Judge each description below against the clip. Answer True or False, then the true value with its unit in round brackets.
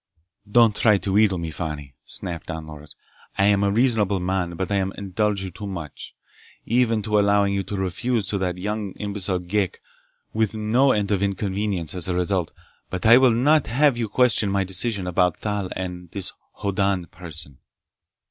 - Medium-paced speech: True (170 wpm)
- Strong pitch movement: False (2.8 semitones)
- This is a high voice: False (100 Hz)